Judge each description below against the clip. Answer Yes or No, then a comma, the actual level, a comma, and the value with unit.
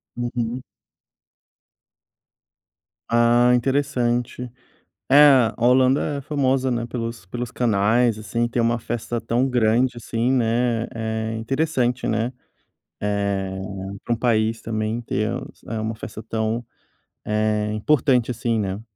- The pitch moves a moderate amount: No, narrow, 2.0 semitones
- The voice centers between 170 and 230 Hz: No, low, 120 Hz